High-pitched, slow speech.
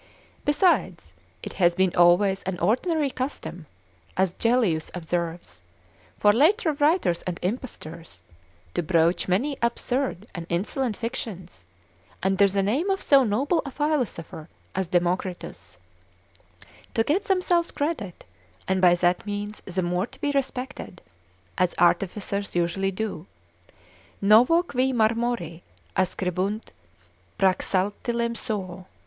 Yes: high, 200 Hz; slow, 115 wpm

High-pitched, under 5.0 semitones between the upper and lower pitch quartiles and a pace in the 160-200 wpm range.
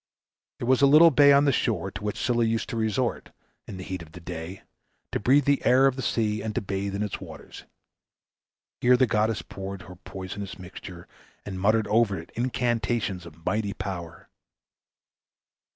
No: low, 105 Hz; average, 4.5 semitones; average, 185 wpm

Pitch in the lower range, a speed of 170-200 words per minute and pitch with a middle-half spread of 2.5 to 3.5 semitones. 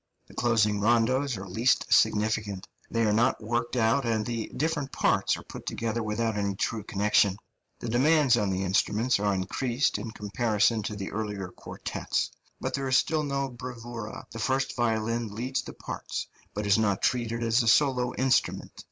Yes: low, 115 Hz; average, 175 wpm; average, 3.0 semitones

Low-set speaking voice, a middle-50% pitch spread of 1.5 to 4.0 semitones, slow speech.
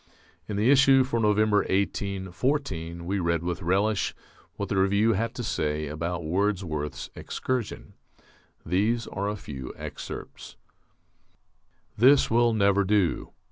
No: low, 100 Hz; average, 4.4 semitones; slow, 125 wpm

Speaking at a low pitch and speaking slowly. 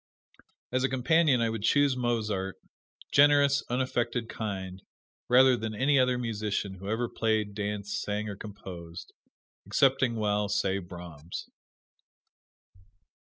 Yes: low, 110 Hz; slow, 115 wpm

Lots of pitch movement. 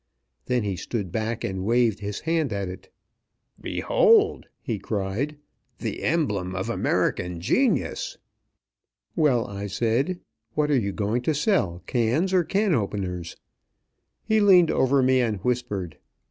Yes: wide, 7.8 semitones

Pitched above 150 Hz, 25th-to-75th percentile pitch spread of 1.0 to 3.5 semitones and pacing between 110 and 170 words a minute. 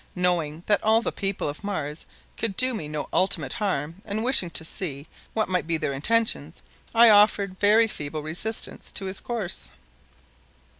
No: high, 190 Hz; wide, 5.5 semitones; average, 165 wpm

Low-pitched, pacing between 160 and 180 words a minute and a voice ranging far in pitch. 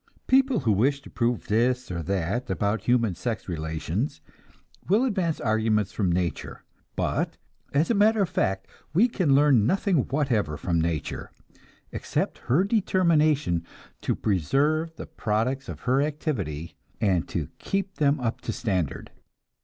No: low, 125 Hz; average, 145 wpm; wide, 8.3 semitones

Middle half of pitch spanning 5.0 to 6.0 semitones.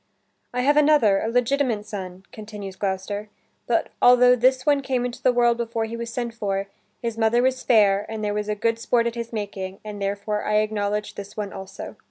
No: average, 2.9 semitones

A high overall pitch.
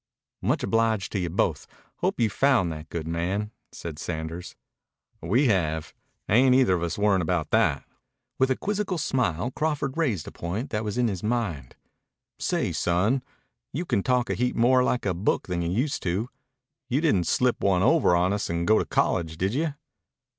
No: low, 105 Hz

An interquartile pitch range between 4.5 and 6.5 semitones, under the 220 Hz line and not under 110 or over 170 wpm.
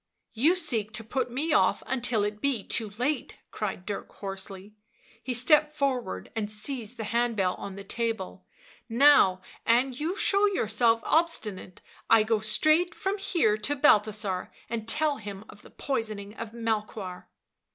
No: average, 4.9 semitones; high, 225 Hz; average, 165 wpm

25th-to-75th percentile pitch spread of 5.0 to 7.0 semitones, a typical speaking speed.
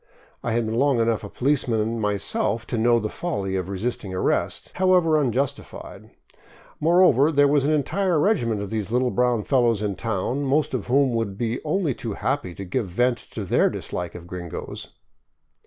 Yes: average, 5.3 semitones; average, 180 wpm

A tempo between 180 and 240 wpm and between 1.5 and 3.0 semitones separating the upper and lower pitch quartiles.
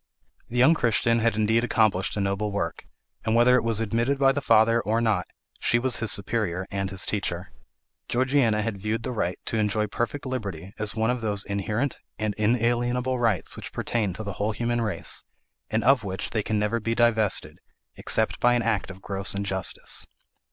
Yes: average, 190 wpm; average, 2.7 semitones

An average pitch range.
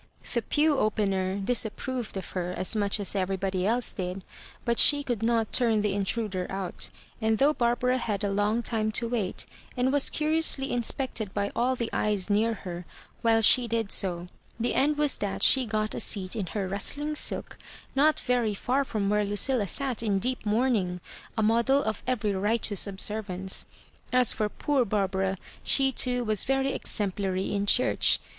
Yes: average, 4.0 semitones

